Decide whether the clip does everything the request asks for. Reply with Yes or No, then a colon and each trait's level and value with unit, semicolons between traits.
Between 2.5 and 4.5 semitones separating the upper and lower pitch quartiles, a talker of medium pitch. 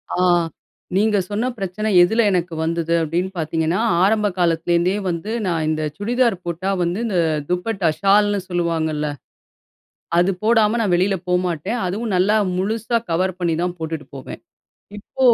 Yes: average, 3.7 semitones; medium, 180 Hz